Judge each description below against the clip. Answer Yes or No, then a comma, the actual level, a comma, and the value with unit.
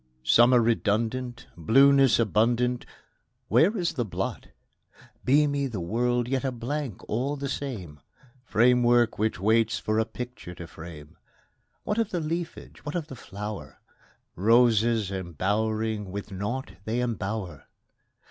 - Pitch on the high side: No, low, 115 Hz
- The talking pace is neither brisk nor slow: No, slow, 130 wpm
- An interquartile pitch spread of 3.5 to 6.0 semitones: Yes, average, 3.8 semitones